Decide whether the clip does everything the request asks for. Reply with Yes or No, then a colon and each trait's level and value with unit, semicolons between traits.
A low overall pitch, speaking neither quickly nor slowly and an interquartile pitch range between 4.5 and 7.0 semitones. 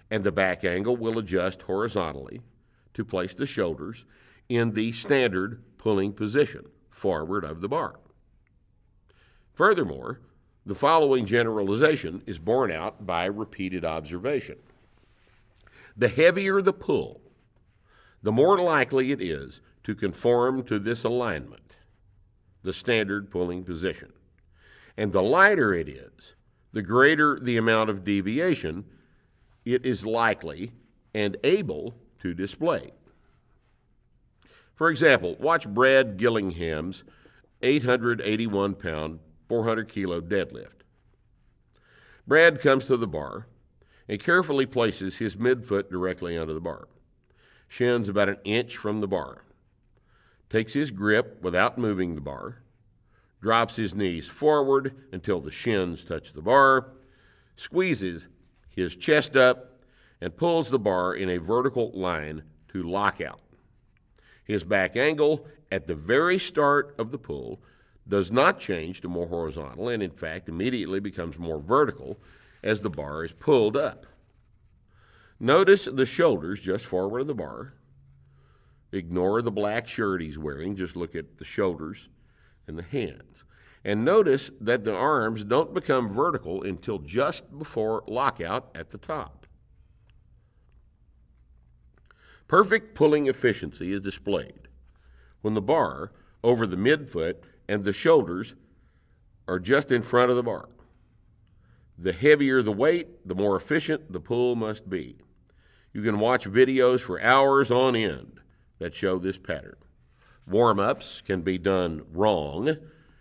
No: low, 105 Hz; slow, 130 wpm; average, 5.2 semitones